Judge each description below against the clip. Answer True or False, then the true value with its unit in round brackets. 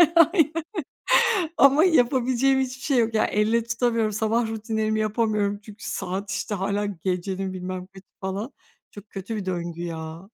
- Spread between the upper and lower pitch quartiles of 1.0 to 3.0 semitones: False (3.6 semitones)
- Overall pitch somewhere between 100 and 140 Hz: False (215 Hz)